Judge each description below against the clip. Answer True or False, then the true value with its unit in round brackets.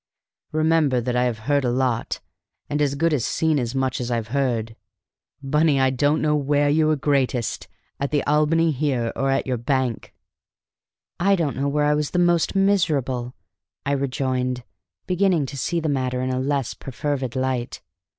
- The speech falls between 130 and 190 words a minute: True (175 wpm)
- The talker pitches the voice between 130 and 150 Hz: True (140 Hz)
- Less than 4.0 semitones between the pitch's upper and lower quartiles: True (2.9 semitones)